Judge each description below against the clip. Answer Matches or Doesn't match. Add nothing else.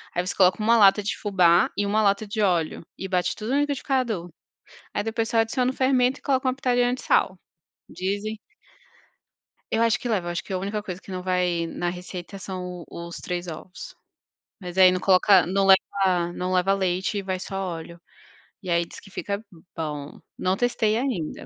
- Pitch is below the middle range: Doesn't match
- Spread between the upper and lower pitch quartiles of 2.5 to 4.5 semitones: Matches